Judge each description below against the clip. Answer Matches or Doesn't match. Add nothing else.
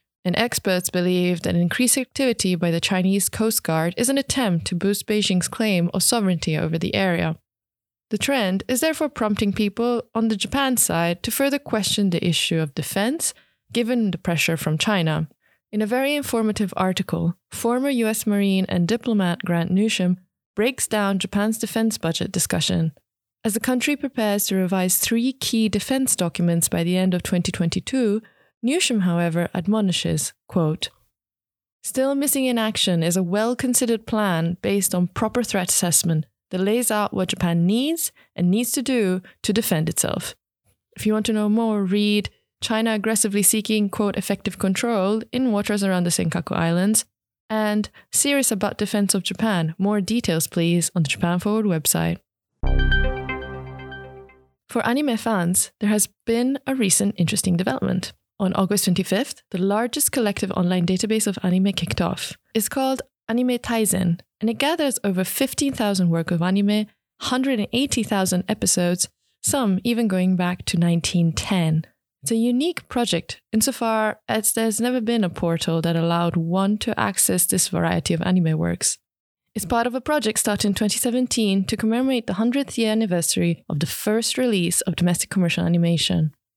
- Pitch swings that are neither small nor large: Matches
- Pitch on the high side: Matches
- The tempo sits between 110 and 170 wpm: Matches